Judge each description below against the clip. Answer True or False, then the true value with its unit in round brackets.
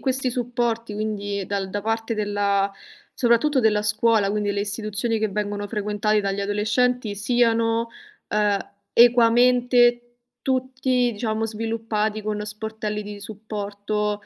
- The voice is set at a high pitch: True (215 Hz)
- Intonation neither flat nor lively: False (2.2 semitones)